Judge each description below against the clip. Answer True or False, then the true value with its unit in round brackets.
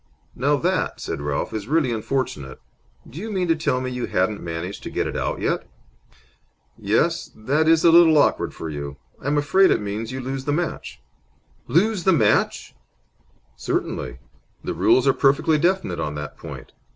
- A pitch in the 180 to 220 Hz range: False (135 Hz)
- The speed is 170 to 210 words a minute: True (175 wpm)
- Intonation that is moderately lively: False (8.3 semitones)